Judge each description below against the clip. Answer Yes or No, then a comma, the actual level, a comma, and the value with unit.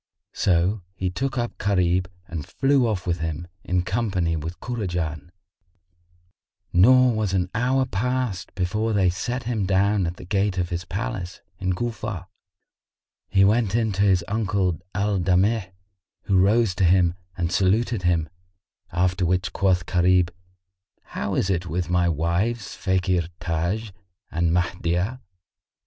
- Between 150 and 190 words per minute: No, average, 140 wpm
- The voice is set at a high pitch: No, very low, 95 Hz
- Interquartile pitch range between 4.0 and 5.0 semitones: No, average, 3.4 semitones